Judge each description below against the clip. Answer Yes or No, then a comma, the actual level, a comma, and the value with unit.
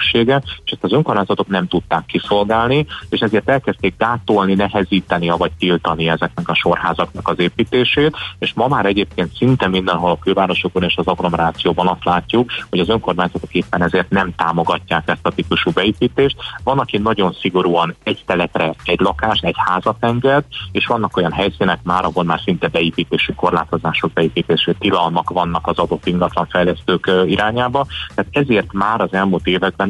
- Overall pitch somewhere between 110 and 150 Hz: No, very low, 95 Hz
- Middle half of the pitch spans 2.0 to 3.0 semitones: No, average, 3.4 semitones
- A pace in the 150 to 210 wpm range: Yes, fast, 155 wpm